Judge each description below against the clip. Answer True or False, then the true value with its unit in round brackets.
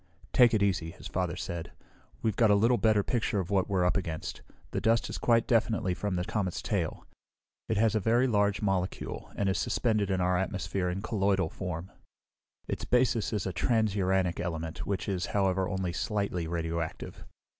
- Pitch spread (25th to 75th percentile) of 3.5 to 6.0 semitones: False (3.1 semitones)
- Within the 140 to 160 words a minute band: False (180 wpm)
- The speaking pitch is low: True (95 Hz)